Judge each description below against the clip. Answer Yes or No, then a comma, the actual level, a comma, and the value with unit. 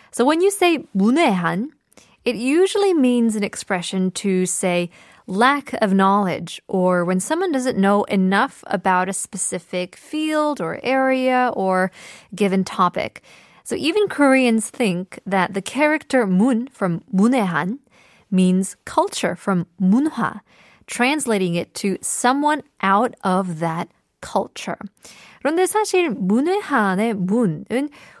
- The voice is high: Yes, high, 215 Hz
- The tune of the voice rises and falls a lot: Yes, wide, 6.0 semitones